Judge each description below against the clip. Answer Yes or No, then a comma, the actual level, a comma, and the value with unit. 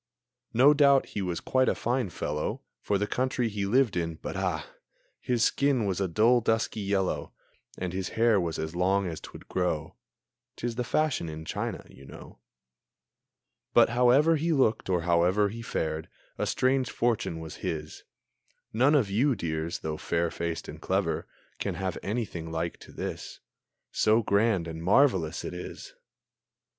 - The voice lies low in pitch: Yes, low, 100 Hz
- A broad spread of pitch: Yes, wide, 6.2 semitones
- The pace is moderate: Yes, average, 165 wpm